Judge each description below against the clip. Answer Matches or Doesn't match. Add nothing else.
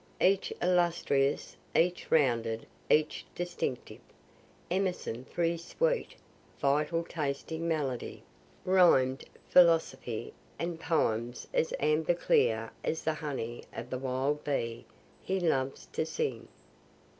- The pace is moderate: Doesn't match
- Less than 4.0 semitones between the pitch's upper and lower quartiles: Doesn't match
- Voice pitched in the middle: Matches